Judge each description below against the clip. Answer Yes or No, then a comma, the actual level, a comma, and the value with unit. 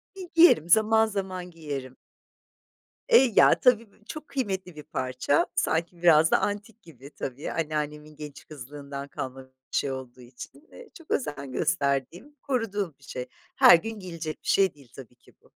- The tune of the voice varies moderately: No, wide, 6.9 semitones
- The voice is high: No, medium, 160 Hz